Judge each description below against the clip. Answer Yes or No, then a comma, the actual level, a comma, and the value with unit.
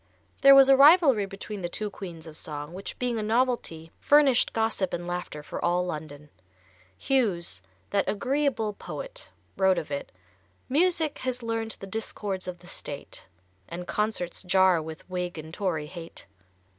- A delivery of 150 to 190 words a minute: Yes, average, 155 wpm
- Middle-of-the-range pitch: No, high, 195 Hz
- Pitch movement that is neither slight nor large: No, wide, 5.9 semitones